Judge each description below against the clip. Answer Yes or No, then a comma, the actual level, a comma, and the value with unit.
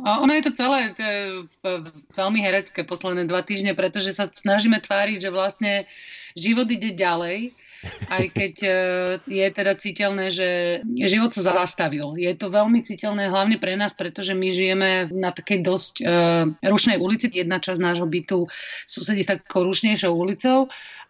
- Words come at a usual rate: Yes, average, 155 wpm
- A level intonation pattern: Yes, narrow, 2.3 semitones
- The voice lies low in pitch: No, high, 195 Hz